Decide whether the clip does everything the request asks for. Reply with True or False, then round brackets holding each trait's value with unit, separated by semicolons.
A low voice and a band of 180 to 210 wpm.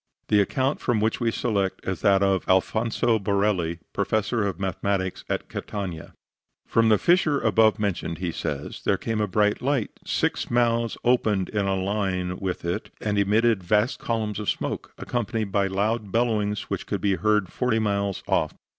False (105 Hz; 170 wpm)